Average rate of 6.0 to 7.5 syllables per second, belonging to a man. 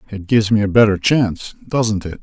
No: 5.7 syllables/s; male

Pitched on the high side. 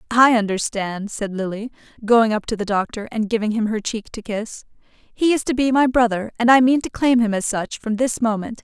Yes: high, 225 Hz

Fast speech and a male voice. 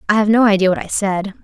No: fast, 290 wpm; female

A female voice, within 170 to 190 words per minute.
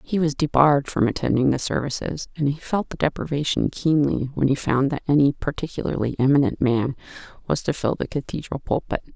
Yes: female; average, 175 wpm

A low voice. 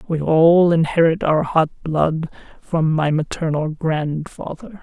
No: medium, 160 Hz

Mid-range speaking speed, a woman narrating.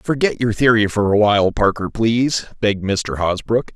No: average, 175 wpm; male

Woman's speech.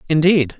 No: male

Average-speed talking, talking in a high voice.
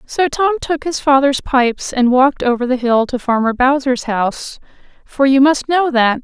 Yes: average, 190 wpm; very high, 265 Hz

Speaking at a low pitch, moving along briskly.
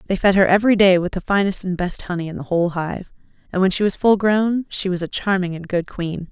No: medium, 185 Hz; fast, 265 wpm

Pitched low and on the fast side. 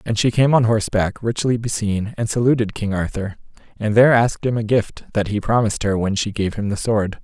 Yes: low, 110 Hz; fast, 225 wpm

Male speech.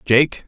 Yes: male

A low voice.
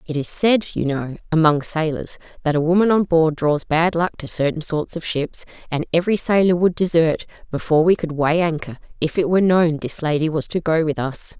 No: medium, 160 Hz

